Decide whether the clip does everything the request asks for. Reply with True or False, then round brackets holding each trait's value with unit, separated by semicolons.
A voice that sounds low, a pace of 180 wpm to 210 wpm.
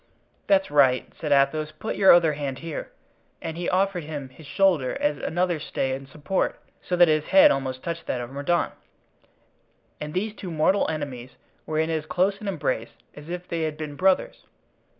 False (155 Hz; 185 wpm)